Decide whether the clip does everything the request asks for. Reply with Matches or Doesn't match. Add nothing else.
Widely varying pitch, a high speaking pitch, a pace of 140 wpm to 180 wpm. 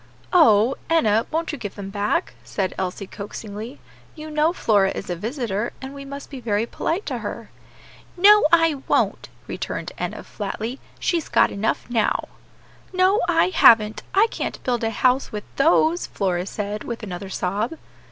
Matches